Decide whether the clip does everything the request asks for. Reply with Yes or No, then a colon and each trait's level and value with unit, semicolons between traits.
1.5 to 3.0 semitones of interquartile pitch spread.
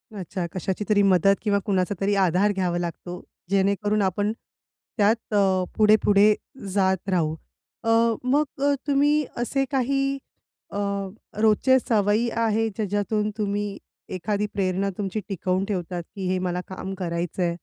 Yes: narrow, 2.5 semitones